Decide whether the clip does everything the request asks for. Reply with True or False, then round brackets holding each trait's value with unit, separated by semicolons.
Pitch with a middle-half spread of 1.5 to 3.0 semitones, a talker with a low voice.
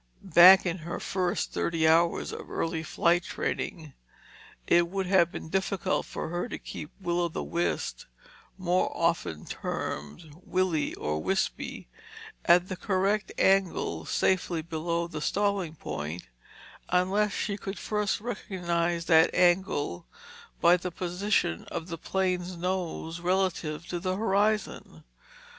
False (2.4 semitones; 175 Hz)